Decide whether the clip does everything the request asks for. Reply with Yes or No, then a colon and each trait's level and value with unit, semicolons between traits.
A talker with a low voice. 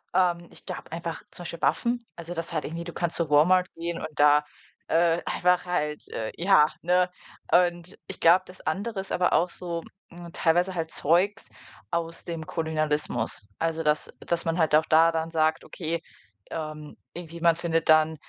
No: medium, 170 Hz